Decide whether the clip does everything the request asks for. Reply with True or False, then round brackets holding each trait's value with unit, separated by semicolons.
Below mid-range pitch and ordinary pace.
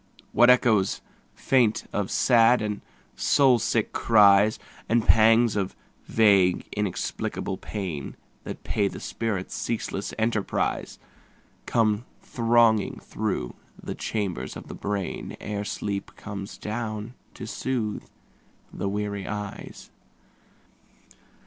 False (105 Hz; 105 wpm)